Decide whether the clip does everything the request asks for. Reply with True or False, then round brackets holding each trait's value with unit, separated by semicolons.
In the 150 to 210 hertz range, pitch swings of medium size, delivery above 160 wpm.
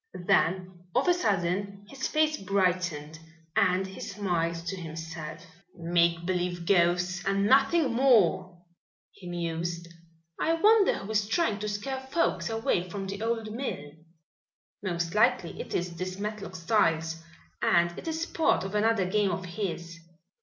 False (185 Hz; 3.8 semitones; 145 wpm)